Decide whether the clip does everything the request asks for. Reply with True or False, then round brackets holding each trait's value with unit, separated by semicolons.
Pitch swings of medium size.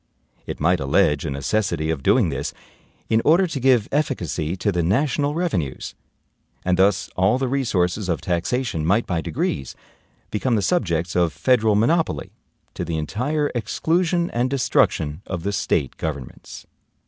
False (8.0 semitones)